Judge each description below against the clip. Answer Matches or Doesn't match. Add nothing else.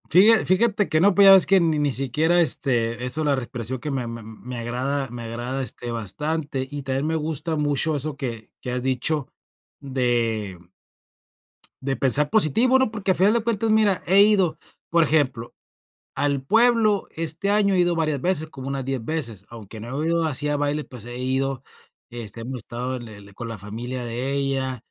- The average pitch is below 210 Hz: Matches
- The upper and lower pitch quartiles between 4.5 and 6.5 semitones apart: Matches